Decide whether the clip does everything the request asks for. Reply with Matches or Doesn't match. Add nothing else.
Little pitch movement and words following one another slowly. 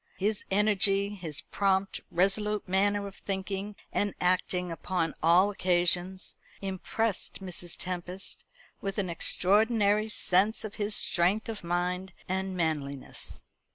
Matches